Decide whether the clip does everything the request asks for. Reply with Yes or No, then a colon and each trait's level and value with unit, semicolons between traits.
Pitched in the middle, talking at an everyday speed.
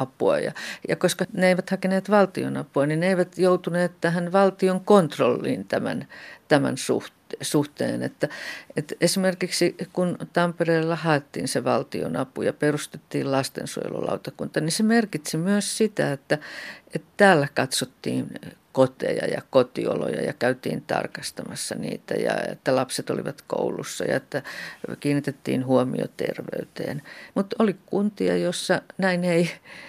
Yes: medium, 175 Hz; average, 120 wpm